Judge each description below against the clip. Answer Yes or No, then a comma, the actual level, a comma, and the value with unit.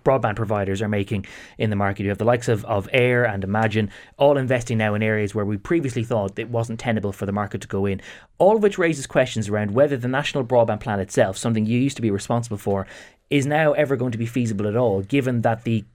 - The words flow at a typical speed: No, fast, 245 wpm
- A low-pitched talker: Yes, low, 115 Hz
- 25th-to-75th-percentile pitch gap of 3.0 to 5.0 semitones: Yes, average, 3.6 semitones